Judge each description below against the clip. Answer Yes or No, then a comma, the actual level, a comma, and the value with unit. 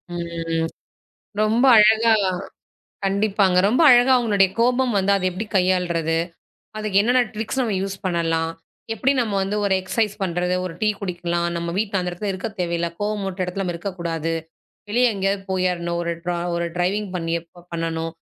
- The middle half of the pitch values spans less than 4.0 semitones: Yes, average, 3.6 semitones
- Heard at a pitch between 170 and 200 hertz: Yes, high, 190 Hz